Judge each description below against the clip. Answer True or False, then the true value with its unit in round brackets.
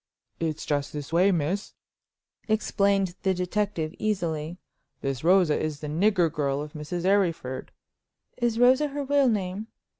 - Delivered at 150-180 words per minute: False (140 wpm)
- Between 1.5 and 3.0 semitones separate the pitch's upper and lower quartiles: False (5.1 semitones)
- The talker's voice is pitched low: False (180 Hz)